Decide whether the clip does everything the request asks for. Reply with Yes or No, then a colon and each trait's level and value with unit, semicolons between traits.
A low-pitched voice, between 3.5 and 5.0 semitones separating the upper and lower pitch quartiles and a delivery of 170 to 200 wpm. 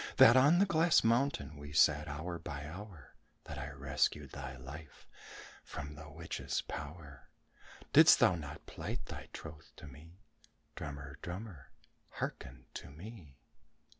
No: very low, 75 Hz; average, 4.3 semitones; slow, 135 wpm